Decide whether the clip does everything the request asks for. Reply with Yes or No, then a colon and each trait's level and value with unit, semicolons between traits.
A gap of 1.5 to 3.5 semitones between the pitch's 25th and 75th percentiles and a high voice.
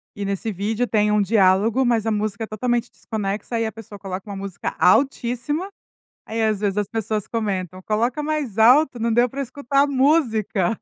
Yes: average, 3.2 semitones; high, 220 Hz